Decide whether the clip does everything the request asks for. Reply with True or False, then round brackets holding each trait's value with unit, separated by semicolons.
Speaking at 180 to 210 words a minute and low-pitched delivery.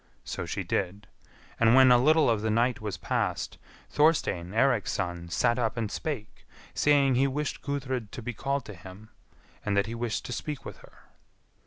True (185 wpm; 120 Hz)